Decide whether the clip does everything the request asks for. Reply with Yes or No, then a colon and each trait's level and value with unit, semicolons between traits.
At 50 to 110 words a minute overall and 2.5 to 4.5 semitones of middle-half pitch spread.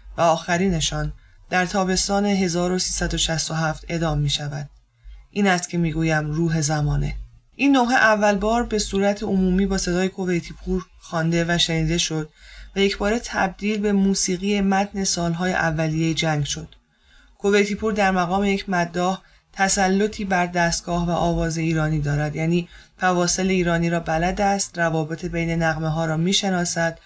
No: average, 145 wpm; average, 3.2 semitones